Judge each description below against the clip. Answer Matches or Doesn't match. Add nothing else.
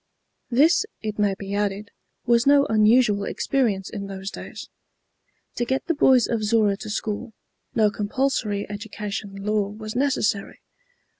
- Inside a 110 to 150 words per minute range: Matches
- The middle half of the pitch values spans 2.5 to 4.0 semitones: Matches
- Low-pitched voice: Doesn't match